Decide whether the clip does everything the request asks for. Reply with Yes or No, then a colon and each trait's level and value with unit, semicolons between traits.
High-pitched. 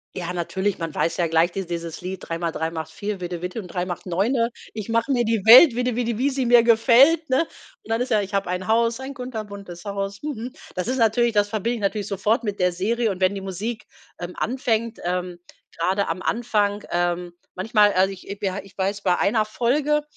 Yes: high, 205 Hz